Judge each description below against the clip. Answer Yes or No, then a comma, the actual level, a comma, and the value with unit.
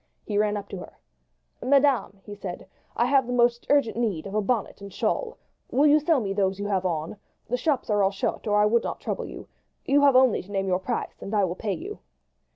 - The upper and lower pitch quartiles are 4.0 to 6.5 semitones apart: Yes, average, 4.8 semitones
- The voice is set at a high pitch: Yes, high, 210 Hz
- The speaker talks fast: Yes, fast, 240 wpm